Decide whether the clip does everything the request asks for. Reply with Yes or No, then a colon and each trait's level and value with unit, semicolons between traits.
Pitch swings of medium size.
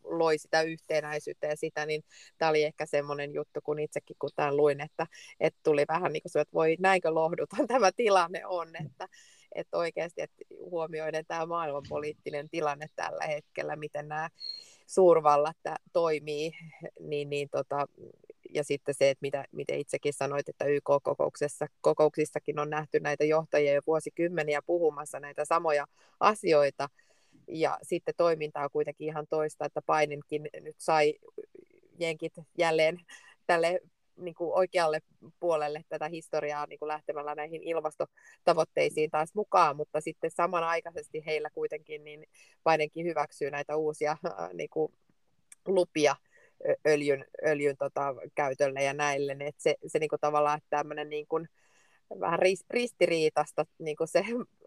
No: narrow, 2.2 semitones